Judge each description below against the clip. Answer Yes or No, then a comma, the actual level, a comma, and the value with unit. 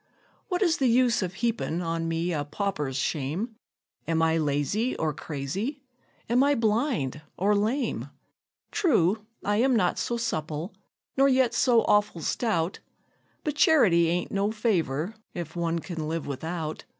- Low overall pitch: No, high, 190 Hz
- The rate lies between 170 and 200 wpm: No, average, 150 wpm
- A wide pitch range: Yes, wide, 6.5 semitones